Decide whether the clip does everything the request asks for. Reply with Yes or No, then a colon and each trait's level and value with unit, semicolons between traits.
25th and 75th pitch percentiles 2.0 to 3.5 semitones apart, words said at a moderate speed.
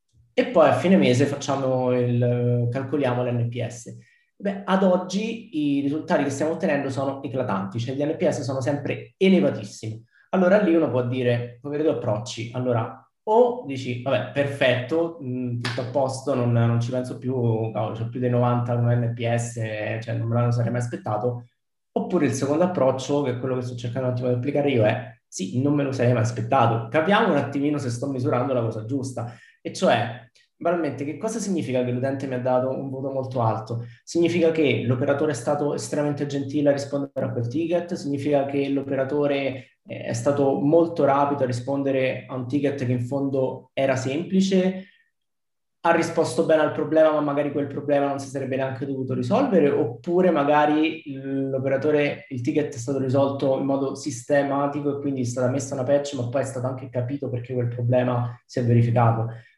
No: average, 2.9 semitones; fast, 180 wpm